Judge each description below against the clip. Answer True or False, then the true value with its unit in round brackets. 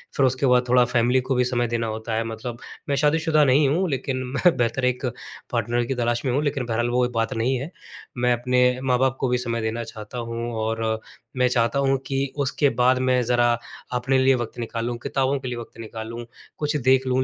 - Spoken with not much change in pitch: True (2.1 semitones)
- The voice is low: True (125 Hz)